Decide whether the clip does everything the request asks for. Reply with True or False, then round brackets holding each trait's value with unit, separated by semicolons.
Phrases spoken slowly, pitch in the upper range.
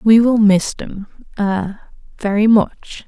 True (100 wpm; 210 Hz)